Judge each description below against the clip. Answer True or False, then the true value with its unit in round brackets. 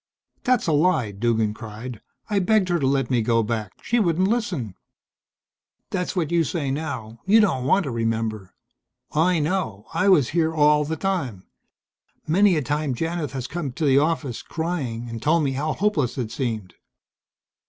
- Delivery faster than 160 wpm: True (175 wpm)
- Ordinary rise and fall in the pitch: False (6.6 semitones)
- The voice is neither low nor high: True (145 Hz)